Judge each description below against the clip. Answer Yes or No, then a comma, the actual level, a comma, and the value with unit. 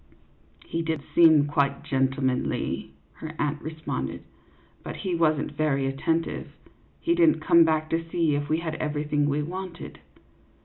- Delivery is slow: No, average, 165 wpm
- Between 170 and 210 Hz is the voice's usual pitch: No, medium, 155 Hz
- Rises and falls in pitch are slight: Yes, narrow, 2.3 semitones